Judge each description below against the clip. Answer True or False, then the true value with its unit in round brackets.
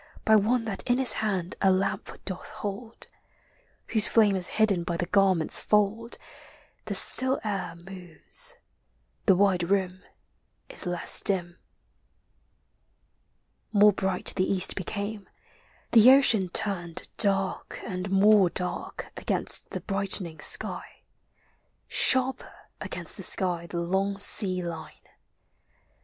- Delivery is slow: True (125 wpm)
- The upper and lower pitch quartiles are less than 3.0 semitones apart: True (2.6 semitones)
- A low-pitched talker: False (195 Hz)